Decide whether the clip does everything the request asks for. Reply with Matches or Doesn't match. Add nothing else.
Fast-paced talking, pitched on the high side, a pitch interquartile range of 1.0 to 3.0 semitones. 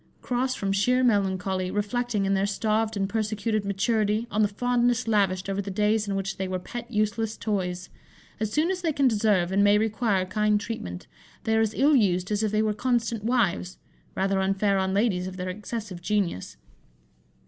Doesn't match